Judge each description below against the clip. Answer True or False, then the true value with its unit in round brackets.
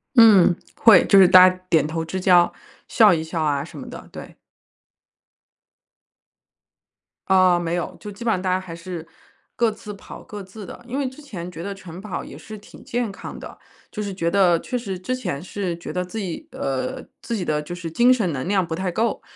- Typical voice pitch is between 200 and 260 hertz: False (185 Hz)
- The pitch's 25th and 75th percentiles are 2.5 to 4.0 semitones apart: True (3.6 semitones)